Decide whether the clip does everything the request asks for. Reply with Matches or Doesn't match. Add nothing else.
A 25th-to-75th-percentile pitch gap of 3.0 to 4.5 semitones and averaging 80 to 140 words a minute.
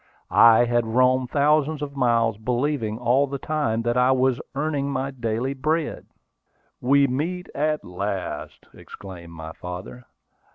Matches